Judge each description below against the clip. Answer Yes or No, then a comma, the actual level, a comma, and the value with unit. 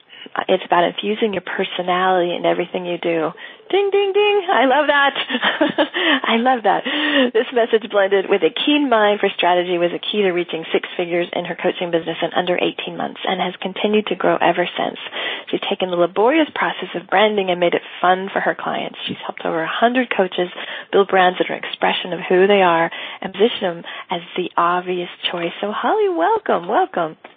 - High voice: Yes, high, 195 Hz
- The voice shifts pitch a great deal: Yes, wide, 5.9 semitones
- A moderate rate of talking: Yes, average, 195 wpm